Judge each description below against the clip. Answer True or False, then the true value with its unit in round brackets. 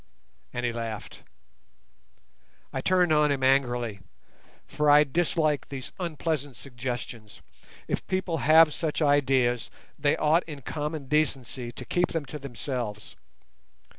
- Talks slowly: True (125 wpm)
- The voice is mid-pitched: True (145 Hz)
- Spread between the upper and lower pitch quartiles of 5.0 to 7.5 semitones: False (4.0 semitones)